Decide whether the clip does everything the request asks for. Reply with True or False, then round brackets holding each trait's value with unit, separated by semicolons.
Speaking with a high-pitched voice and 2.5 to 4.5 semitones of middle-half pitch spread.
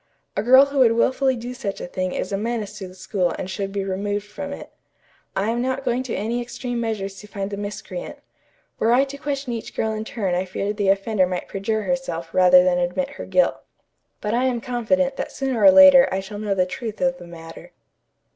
False (220 Hz; 4.9 semitones)